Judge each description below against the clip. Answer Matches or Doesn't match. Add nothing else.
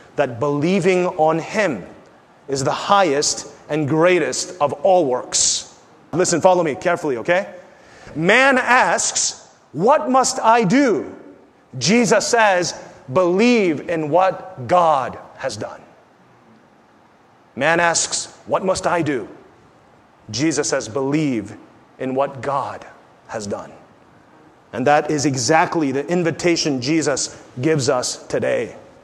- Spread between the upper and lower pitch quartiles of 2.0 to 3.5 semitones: Doesn't match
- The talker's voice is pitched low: Doesn't match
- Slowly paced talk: Matches